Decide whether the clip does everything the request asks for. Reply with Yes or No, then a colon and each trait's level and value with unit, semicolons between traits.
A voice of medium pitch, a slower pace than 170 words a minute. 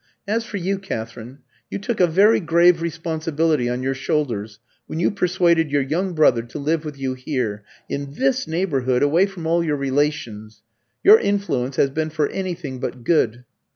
No: medium, 155 Hz; average, 175 wpm